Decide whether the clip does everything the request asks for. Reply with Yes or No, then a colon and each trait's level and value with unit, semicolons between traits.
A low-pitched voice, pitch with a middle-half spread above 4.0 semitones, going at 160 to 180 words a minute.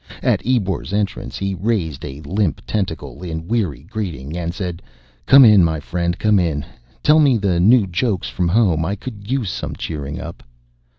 Yes: very low, 90 Hz; average, 4.6 semitones; average, 175 wpm